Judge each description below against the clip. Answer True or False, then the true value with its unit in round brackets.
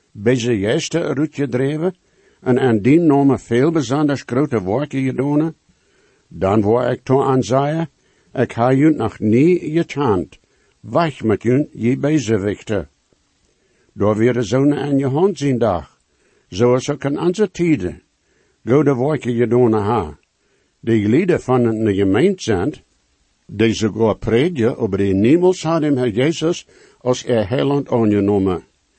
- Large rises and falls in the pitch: False (4.8 semitones)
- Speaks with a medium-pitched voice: False (130 Hz)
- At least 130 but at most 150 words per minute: True (145 wpm)